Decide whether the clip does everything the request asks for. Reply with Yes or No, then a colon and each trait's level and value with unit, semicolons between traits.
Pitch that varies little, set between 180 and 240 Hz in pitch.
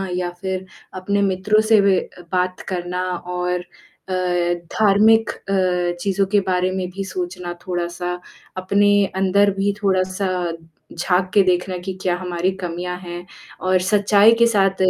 Yes: narrow, 1.7 semitones; medium, 185 Hz